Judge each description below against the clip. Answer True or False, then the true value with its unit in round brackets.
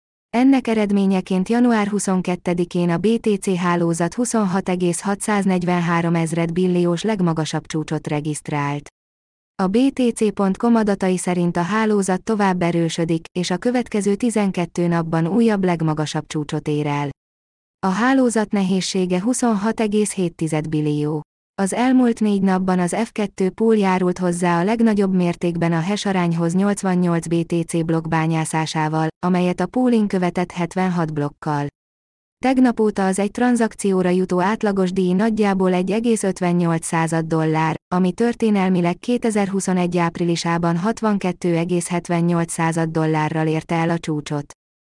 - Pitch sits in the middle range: True (180 Hz)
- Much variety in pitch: False (3.7 semitones)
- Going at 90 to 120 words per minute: True (110 wpm)